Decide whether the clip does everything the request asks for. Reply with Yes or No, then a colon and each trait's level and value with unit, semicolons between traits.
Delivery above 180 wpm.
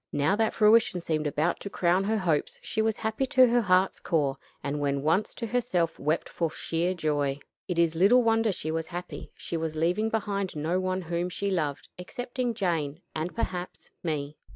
Yes: average, 190 wpm